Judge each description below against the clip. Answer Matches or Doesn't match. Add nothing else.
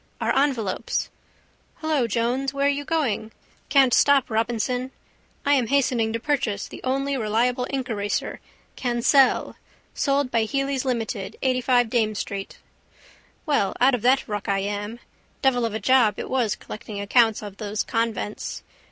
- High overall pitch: Matches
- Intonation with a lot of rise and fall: Doesn't match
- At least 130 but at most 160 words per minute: Matches